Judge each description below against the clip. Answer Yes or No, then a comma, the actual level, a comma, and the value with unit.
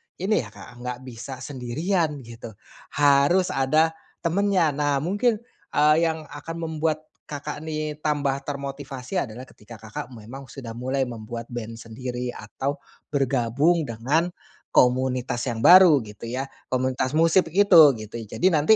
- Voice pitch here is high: No, medium, 140 Hz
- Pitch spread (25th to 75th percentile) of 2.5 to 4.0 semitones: No, average, 4.4 semitones